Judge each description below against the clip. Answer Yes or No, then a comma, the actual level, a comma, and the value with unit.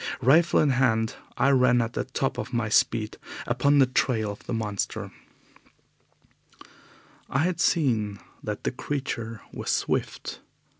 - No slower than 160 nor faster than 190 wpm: No, average, 140 wpm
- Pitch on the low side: Yes, low, 125 Hz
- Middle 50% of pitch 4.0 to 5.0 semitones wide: No, average, 3.4 semitones